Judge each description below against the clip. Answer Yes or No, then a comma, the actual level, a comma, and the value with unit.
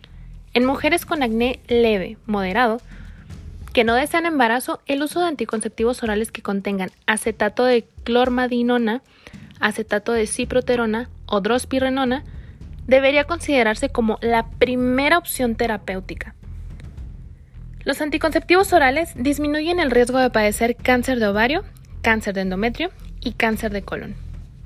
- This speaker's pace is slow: Yes, slow, 120 wpm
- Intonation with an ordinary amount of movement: Yes, average, 3.4 semitones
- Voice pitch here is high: Yes, high, 240 Hz